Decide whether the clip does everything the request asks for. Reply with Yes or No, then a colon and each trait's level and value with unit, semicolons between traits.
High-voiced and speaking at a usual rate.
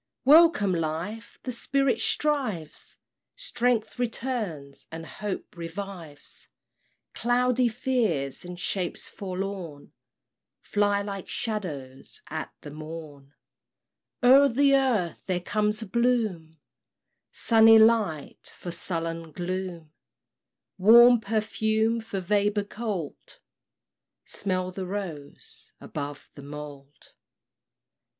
No: high, 200 Hz; slow, 95 wpm